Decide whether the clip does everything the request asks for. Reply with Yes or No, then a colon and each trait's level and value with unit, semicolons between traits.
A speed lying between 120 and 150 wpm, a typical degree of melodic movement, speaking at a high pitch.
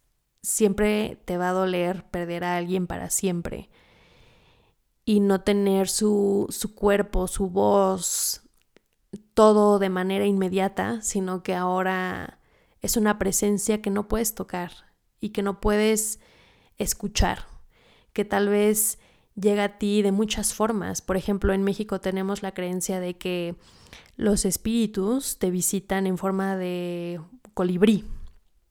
No: average, 130 wpm; narrow, 2.0 semitones; high, 195 Hz